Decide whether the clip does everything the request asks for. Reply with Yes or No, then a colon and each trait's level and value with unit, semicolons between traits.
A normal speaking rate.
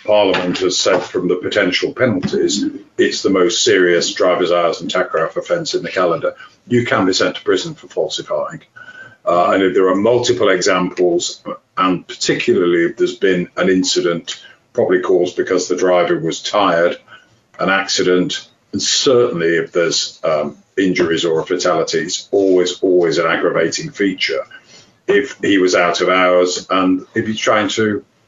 Yes: average, 155 wpm